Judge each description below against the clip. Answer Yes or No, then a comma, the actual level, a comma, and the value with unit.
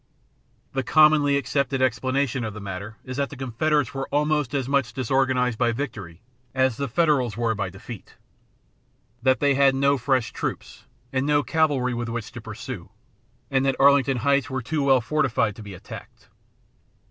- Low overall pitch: Yes, low, 130 Hz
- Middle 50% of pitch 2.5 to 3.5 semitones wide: Yes, average, 3.1 semitones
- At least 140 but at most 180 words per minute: Yes, average, 170 wpm